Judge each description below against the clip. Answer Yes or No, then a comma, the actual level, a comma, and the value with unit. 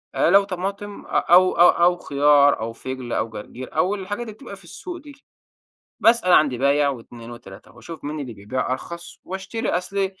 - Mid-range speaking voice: Yes, medium, 170 Hz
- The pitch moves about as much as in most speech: No, wide, 7.2 semitones